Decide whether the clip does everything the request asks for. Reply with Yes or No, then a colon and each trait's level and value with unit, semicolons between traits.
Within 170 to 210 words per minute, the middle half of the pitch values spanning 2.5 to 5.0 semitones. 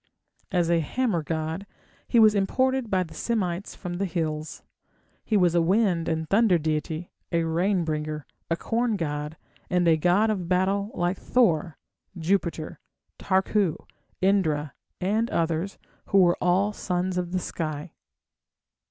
No: average, 145 wpm; average, 3.5 semitones